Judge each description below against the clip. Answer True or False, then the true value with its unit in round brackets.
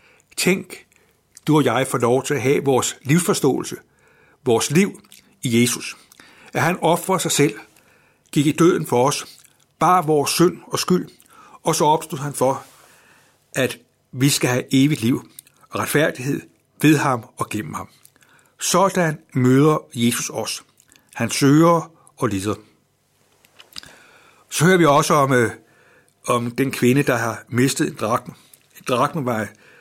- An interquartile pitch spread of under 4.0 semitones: False (4.4 semitones)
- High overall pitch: False (140 Hz)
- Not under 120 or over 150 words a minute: True (145 wpm)